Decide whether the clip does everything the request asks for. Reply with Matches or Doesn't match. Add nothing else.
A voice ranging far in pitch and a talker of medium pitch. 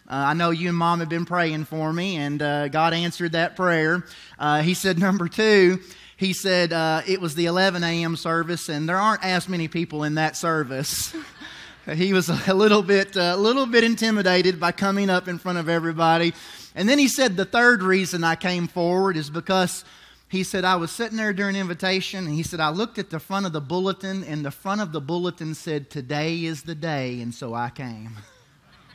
Doesn't match